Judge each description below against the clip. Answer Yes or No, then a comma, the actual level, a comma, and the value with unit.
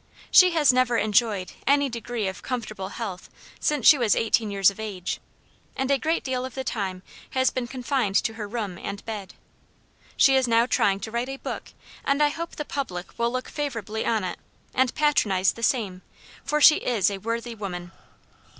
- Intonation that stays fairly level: No, average, 4.7 semitones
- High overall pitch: Yes, high, 235 Hz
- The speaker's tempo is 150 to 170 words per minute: No, average, 190 wpm